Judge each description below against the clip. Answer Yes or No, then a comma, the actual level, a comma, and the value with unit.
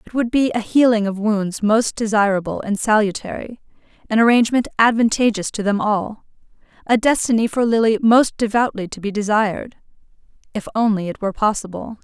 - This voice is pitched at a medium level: No, high, 215 Hz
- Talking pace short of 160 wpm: Yes, average, 150 wpm